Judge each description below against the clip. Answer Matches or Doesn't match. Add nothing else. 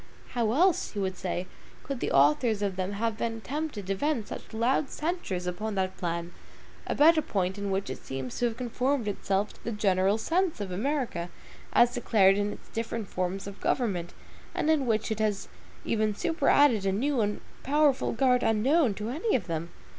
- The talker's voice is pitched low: Doesn't match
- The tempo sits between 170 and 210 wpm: Matches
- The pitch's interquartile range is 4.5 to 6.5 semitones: Matches